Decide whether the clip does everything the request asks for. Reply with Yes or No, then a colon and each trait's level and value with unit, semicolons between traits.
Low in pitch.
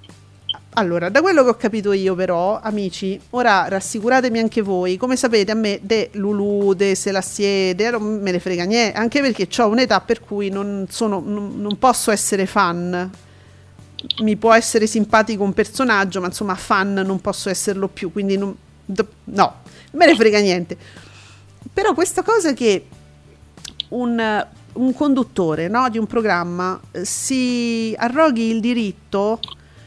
No: high, 205 Hz